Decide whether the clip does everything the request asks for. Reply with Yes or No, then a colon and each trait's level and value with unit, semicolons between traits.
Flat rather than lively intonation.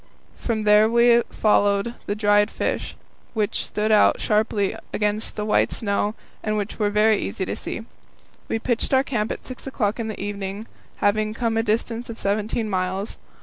Yes: narrow, 1.6 semitones